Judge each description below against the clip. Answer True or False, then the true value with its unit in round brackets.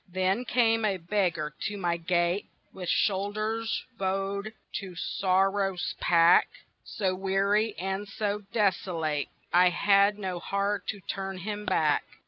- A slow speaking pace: True (125 wpm)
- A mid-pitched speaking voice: False (195 Hz)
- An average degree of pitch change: False (2.2 semitones)